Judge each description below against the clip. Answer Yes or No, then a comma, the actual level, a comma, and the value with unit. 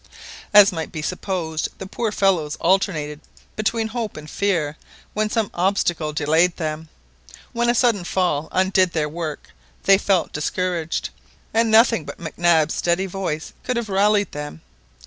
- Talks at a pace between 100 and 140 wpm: No, average, 150 wpm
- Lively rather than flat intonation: No, average, 4.4 semitones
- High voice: No, medium, 180 Hz